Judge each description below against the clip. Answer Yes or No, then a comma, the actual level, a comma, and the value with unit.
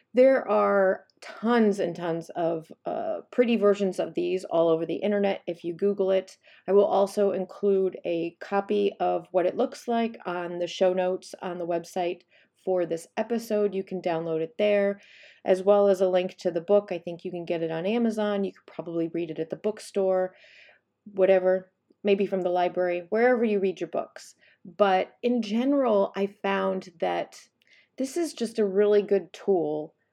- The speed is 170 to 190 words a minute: Yes, average, 185 wpm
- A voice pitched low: No, high, 195 Hz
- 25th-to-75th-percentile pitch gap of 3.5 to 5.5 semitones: No, average, 2.7 semitones